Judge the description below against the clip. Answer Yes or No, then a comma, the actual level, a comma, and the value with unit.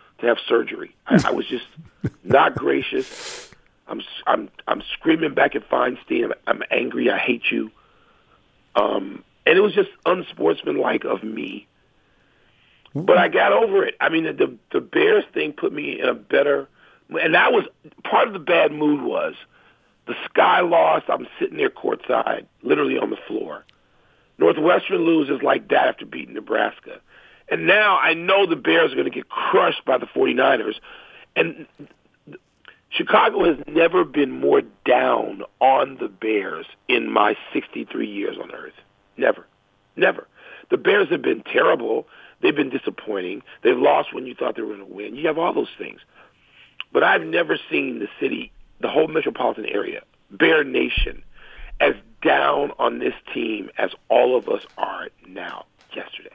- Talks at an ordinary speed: Yes, average, 165 wpm